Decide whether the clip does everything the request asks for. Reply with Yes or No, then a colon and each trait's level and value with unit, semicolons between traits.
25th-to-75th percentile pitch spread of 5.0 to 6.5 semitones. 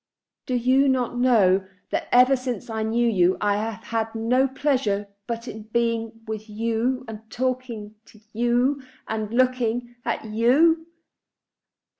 No: narrow, 2.5 semitones